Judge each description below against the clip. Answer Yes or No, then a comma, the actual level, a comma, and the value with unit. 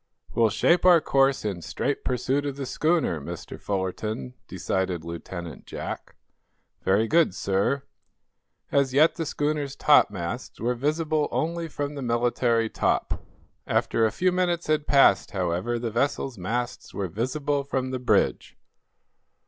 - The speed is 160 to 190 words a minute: No, average, 140 wpm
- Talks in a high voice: No, low, 125 Hz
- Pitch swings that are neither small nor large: No, wide, 6.3 semitones